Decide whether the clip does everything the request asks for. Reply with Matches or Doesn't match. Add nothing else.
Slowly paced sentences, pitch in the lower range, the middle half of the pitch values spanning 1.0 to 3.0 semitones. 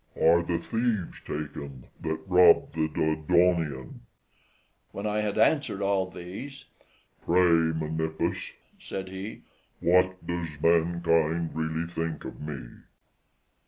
Matches